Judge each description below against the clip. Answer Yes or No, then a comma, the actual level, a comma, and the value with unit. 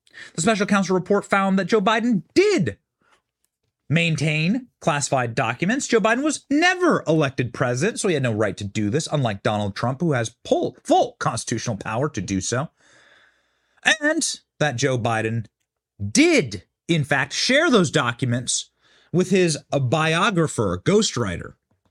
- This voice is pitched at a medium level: Yes, medium, 155 Hz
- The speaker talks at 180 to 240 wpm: No, average, 145 wpm